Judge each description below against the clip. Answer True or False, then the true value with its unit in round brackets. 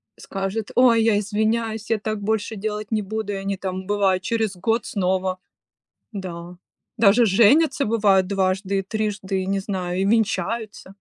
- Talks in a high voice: True (205 Hz)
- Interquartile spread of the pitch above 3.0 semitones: False (2.5 semitones)